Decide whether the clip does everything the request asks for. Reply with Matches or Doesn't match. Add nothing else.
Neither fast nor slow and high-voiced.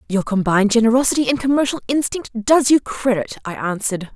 Matches